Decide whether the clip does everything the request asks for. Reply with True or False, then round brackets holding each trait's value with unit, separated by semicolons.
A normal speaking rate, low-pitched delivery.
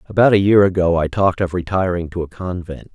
False (225 wpm; 90 Hz)